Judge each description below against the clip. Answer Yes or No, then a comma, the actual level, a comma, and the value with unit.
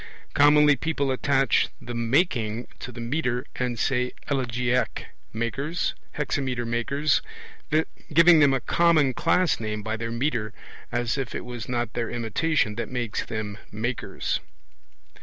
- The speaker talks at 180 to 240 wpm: No, slow, 135 wpm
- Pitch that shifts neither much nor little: Yes, average, 3.5 semitones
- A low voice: Yes, low, 125 Hz